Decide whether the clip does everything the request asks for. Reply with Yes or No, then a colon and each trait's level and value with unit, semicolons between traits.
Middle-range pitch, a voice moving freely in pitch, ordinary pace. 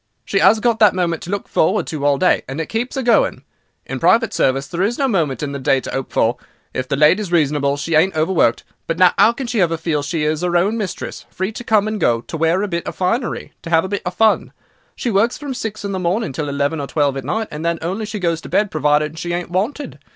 No: medium, 175 Hz; wide, 5.7 semitones; fast, 265 wpm